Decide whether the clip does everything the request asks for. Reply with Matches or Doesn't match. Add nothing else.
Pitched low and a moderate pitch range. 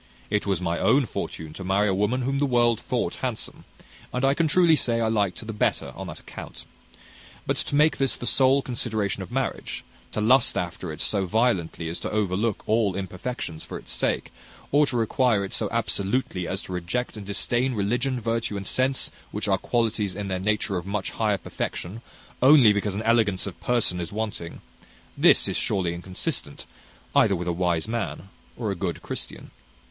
Matches